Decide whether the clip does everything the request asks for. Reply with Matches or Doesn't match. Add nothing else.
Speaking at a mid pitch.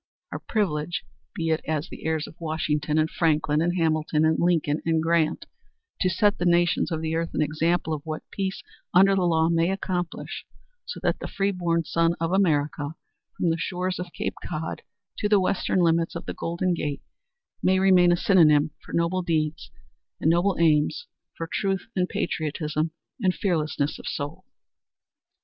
Matches